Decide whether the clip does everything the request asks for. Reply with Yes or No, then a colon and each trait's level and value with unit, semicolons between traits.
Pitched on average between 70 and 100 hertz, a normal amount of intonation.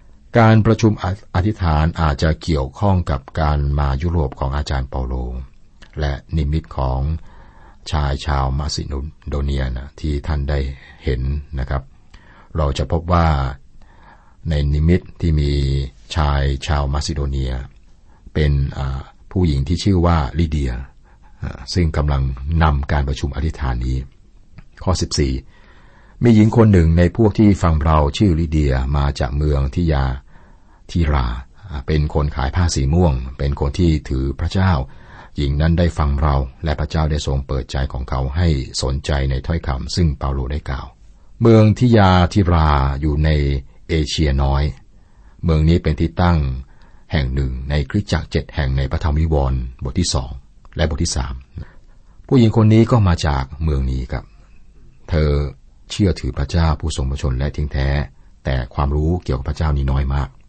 Yes: very low, 75 Hz; average, 3.8 semitones